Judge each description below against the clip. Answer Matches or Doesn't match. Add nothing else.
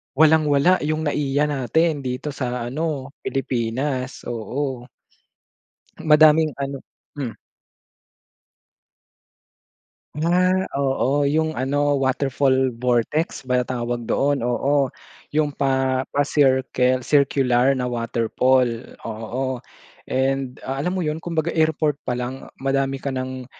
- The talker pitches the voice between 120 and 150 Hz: Matches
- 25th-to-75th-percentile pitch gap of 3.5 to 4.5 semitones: Doesn't match